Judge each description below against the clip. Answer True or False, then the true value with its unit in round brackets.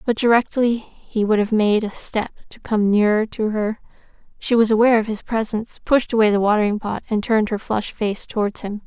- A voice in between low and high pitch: False (215 Hz)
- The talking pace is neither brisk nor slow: False (210 wpm)